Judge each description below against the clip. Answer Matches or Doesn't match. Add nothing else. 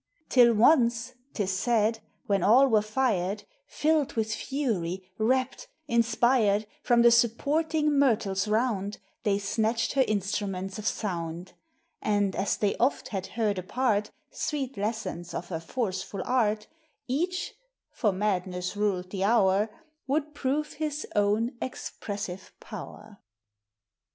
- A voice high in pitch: Matches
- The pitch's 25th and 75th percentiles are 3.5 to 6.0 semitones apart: Matches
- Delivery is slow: Matches